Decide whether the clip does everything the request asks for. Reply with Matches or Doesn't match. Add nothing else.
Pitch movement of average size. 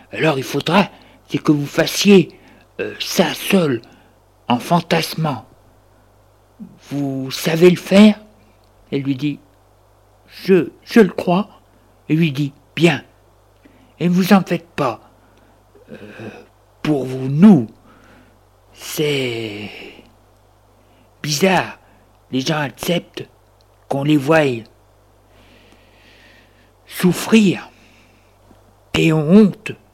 Doesn't match